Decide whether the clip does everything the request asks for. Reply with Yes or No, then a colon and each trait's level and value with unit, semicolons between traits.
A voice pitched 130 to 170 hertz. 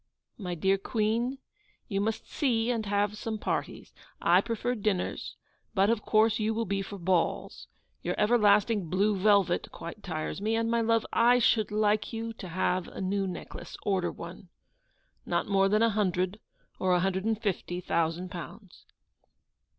No: high, 205 Hz